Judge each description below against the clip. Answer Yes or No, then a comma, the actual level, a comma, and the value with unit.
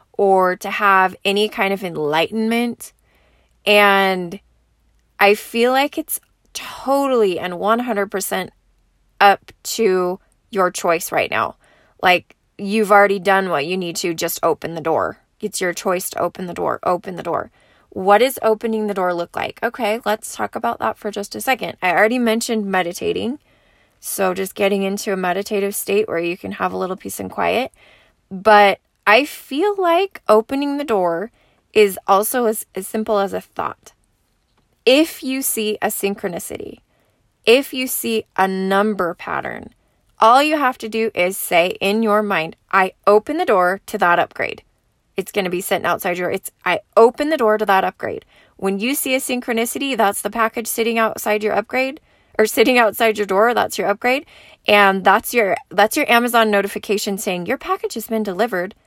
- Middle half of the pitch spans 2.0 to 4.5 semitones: Yes, average, 3.4 semitones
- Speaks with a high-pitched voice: Yes, high, 205 Hz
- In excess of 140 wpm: Yes, average, 175 wpm